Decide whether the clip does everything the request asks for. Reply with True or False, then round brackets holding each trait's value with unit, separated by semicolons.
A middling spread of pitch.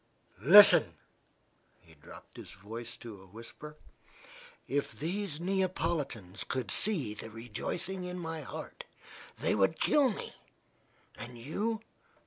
False (8.7 semitones)